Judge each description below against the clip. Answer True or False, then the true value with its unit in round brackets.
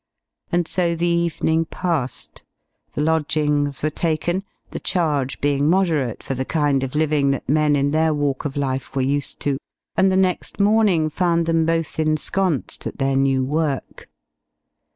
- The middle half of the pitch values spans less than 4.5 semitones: True (3.2 semitones)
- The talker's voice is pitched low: False (155 Hz)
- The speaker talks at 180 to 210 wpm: False (160 wpm)